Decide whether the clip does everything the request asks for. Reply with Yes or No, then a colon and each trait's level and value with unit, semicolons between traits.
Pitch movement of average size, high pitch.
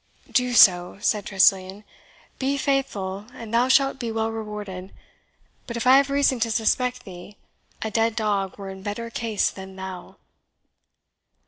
Yes: average, 4.1 semitones; high, 220 Hz